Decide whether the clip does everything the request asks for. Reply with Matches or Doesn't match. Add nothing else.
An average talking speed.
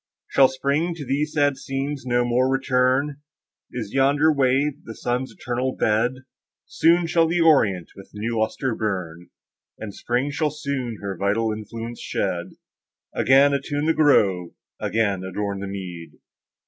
Matches